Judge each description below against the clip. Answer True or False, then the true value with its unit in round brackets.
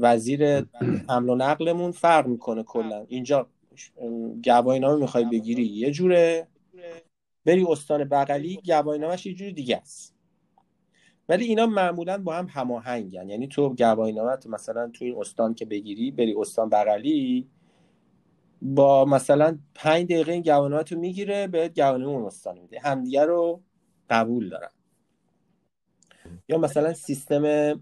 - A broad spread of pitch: True (5.8 semitones)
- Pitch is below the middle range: False (145 Hz)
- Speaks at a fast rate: False (130 wpm)